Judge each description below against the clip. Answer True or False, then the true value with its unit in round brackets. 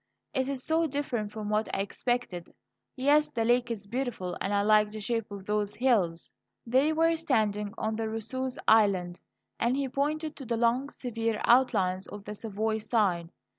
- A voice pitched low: False (225 Hz)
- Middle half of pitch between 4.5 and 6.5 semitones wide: False (3.9 semitones)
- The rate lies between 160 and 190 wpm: True (170 wpm)